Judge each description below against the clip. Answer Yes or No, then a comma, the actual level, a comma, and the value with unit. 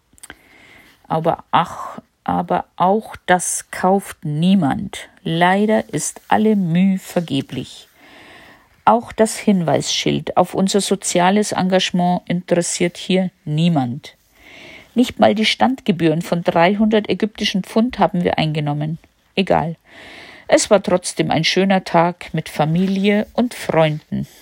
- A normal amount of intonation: Yes, average, 3.8 semitones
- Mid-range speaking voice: Yes, medium, 180 Hz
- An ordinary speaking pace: No, slow, 110 wpm